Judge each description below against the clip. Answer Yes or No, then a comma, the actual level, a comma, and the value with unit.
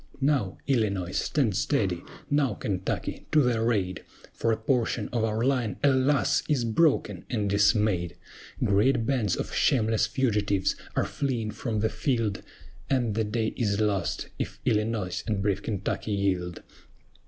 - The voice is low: Yes, low, 110 Hz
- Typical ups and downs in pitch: Yes, average, 3.6 semitones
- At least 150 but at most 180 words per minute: No, average, 140 wpm